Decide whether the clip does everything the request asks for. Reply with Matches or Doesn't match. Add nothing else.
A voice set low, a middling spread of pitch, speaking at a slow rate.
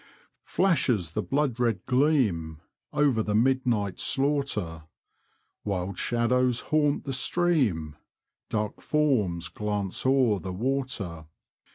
Doesn't match